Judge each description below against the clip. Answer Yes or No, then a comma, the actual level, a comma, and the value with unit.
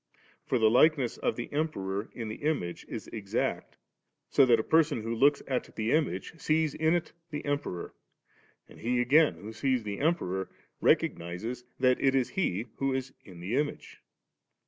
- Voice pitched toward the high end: No, low, 125 Hz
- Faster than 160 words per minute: Yes, average, 170 wpm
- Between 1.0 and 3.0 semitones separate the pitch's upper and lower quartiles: No, average, 5.0 semitones